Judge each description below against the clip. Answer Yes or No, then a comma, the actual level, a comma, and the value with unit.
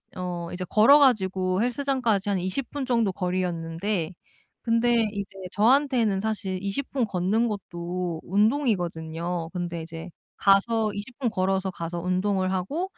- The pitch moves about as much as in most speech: Yes, average, 4.4 semitones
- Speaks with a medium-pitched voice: No, high, 195 Hz